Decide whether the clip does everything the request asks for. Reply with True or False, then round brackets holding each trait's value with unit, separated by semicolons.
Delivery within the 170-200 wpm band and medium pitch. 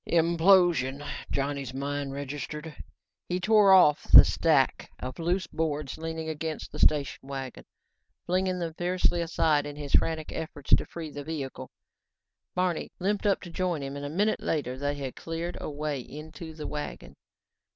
False (160 wpm; 155 Hz)